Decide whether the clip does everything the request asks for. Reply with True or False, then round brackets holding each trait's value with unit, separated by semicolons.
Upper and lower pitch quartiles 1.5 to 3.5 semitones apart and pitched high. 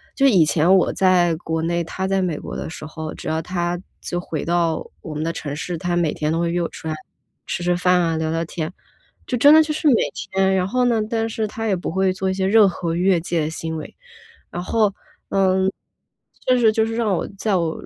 False (3.0 semitones; 180 Hz)